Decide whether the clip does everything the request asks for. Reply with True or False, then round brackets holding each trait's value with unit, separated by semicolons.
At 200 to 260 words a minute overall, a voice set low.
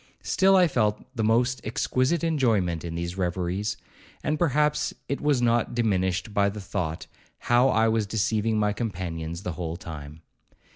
False (155 wpm; 105 Hz)